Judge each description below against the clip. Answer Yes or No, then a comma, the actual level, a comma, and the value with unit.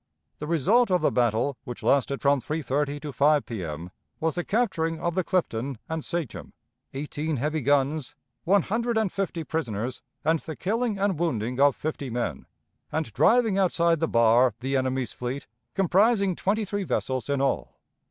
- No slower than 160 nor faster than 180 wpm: Yes, average, 165 wpm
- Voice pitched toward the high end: No, medium, 155 Hz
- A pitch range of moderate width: No, wide, 5.9 semitones